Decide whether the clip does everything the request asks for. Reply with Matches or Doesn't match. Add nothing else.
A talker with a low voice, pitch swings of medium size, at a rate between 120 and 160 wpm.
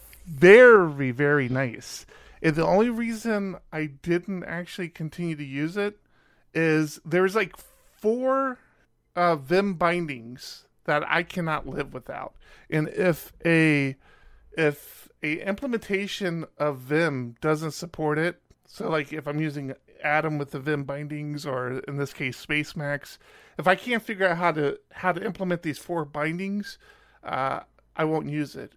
Doesn't match